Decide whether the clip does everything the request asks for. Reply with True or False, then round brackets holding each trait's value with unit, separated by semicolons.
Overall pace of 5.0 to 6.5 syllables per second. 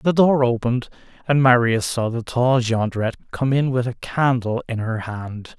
False (4.7 syllables/s)